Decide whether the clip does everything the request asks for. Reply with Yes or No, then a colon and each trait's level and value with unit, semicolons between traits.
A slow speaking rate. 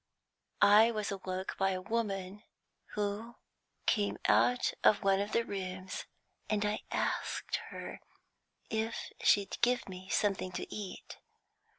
Yes: slow, 125 wpm